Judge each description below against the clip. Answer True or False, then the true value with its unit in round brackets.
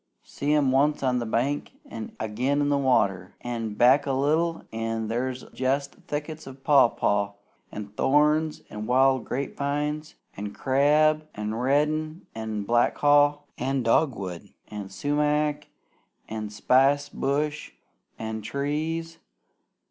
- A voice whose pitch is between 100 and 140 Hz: True (135 Hz)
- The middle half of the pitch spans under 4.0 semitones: False (4.6 semitones)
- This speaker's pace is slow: True (125 wpm)